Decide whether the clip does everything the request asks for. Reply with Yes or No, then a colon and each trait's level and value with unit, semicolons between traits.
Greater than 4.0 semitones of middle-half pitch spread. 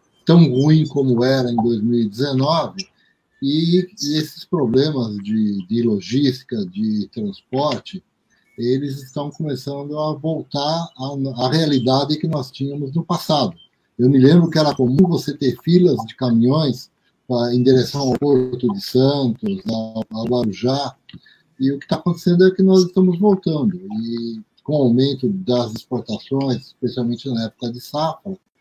Yes: average, 5.1 semitones